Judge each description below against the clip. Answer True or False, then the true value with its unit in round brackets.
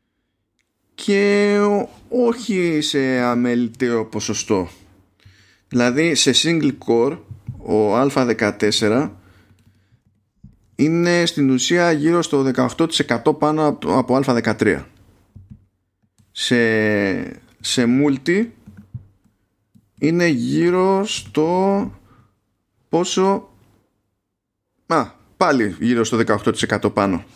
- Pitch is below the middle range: True (120 Hz)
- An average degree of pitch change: False (6.5 semitones)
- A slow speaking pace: True (70 wpm)